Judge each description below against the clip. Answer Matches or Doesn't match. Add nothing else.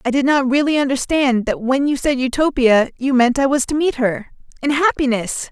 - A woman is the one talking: Matches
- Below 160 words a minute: Doesn't match